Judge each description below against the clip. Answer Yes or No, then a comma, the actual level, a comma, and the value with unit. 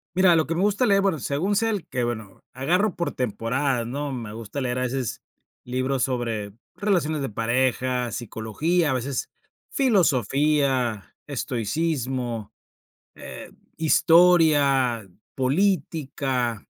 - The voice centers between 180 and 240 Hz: No, low, 135 Hz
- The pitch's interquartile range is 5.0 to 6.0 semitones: Yes, average, 5.3 semitones